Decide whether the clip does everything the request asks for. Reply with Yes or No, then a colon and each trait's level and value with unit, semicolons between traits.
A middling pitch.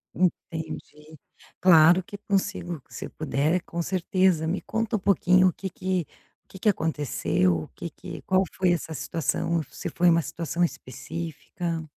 Yes: medium, 170 Hz